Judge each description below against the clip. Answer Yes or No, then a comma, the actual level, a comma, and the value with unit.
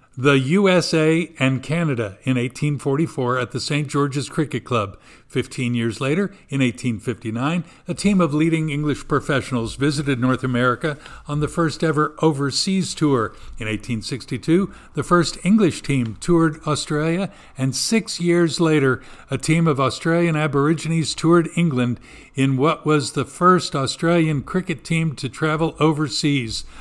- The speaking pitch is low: No, medium, 145 Hz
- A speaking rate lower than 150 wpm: Yes, average, 140 wpm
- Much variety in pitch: No, average, 4.1 semitones